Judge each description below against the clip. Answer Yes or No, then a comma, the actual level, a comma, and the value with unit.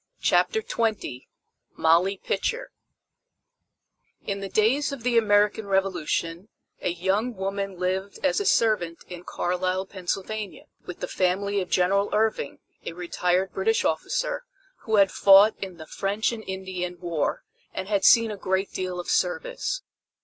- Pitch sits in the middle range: No, high, 195 Hz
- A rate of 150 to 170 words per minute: No, average, 140 wpm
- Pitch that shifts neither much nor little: Yes, average, 3.2 semitones